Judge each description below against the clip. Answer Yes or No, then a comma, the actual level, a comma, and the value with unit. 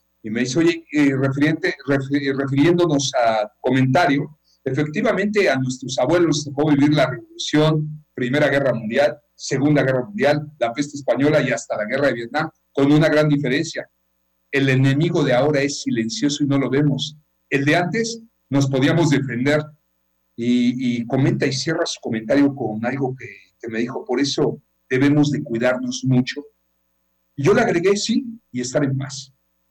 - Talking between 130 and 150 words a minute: No, average, 165 wpm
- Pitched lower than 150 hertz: Yes, medium, 140 Hz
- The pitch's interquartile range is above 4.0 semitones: No, average, 3.1 semitones